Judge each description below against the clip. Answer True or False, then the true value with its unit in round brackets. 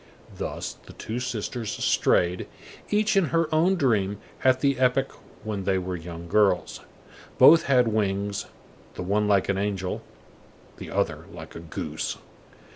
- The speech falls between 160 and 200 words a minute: False (145 wpm)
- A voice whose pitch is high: False (105 Hz)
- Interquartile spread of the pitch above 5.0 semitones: True (5.4 semitones)